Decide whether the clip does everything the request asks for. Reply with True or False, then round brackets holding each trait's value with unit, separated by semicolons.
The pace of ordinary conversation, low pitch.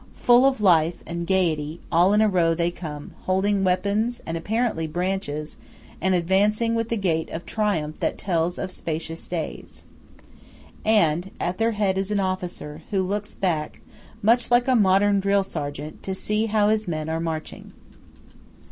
False (165 wpm; 185 Hz)